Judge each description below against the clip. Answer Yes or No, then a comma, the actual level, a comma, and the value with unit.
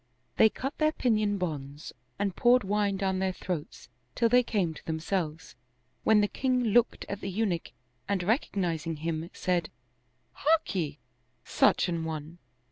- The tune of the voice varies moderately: Yes, average, 5.0 semitones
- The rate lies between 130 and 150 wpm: Yes, average, 145 wpm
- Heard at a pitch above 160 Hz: Yes, high, 190 Hz